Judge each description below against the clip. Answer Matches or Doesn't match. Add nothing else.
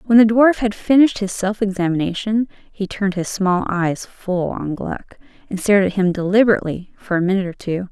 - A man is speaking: Doesn't match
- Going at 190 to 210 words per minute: Matches